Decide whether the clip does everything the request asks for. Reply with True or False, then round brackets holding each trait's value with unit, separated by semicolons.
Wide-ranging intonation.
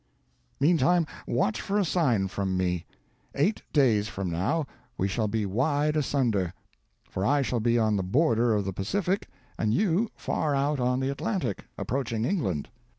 True (7.0 semitones)